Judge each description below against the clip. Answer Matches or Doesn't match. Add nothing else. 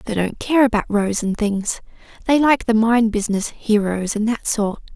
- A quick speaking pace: Doesn't match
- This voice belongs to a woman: Matches